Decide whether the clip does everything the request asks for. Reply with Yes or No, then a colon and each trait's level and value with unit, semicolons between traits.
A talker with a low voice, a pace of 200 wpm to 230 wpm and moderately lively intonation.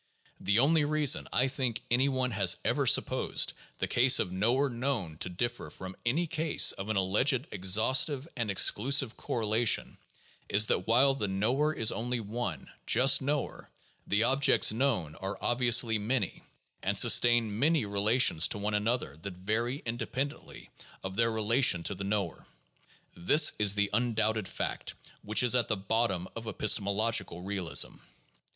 No: low, 115 Hz; average, 155 wpm; average, 4.2 semitones